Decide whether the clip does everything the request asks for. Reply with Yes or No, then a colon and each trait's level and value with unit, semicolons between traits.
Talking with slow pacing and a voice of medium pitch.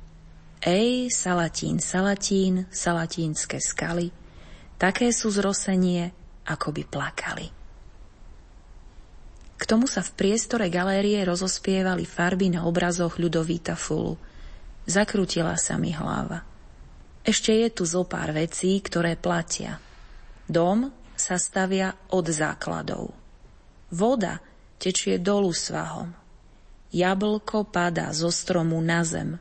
Yes: slow, 100 wpm; medium, 180 Hz